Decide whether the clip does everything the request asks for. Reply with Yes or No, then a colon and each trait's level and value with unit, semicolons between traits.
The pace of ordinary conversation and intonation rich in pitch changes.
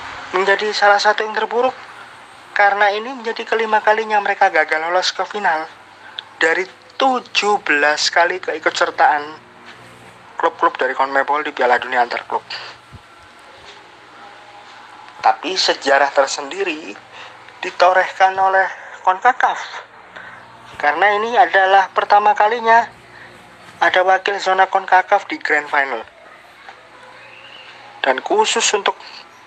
No: average, 100 wpm; average, 3.3 semitones